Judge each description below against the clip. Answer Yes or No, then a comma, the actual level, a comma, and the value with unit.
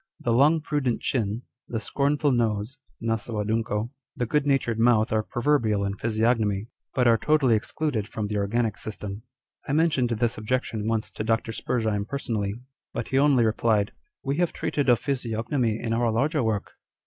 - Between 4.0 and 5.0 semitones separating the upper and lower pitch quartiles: No, average, 3.5 semitones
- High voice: No, low, 115 Hz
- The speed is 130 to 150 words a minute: No, average, 170 wpm